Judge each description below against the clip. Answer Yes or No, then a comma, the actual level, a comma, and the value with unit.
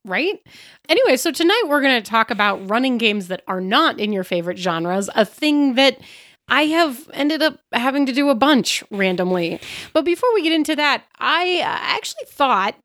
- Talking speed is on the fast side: No, average, 185 wpm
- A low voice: No, very high, 275 Hz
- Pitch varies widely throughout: Yes, wide, 7.5 semitones